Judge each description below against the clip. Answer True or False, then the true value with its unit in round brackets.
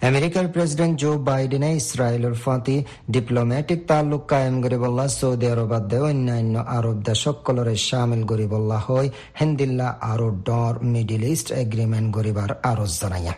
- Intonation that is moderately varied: True (3.4 semitones)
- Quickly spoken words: True (130 wpm)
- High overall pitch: False (125 Hz)